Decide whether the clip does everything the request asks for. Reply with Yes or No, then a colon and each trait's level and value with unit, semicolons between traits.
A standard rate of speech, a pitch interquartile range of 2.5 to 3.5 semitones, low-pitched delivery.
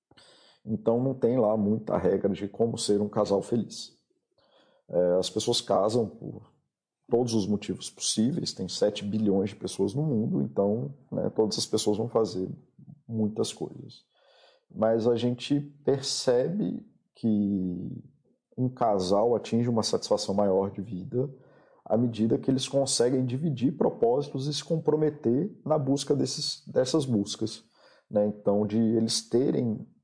No: average, 140 wpm; average, 4.6 semitones; low, 115 Hz